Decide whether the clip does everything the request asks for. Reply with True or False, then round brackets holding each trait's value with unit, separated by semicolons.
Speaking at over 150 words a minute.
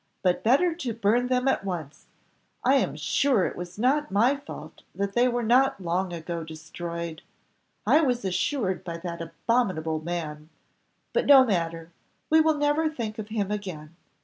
True (165 wpm)